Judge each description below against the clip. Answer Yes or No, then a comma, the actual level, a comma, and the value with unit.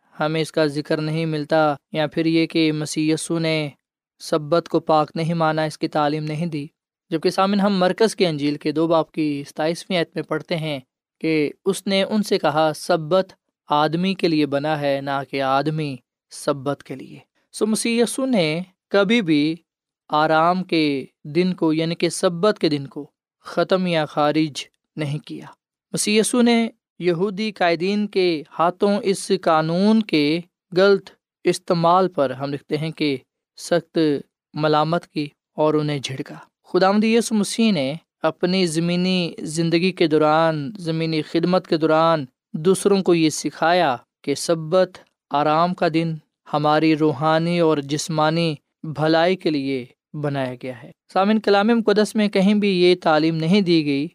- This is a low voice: No, medium, 165 Hz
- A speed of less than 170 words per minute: Yes, average, 155 wpm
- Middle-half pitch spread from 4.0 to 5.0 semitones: No, average, 3.3 semitones